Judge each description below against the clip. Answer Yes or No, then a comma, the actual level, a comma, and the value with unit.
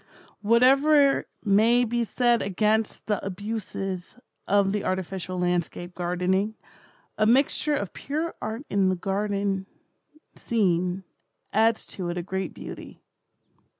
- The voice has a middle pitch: No, high, 200 Hz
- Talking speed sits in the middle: No, slow, 115 wpm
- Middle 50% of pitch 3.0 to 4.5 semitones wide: Yes, average, 3.7 semitones